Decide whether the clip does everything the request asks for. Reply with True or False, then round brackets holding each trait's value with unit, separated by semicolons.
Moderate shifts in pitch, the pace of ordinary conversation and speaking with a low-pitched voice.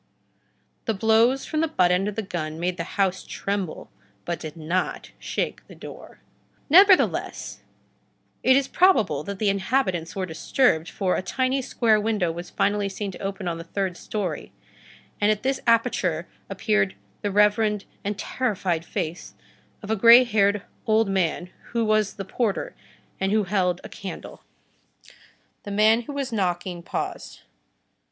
False (3.7 semitones; 155 wpm; 200 Hz)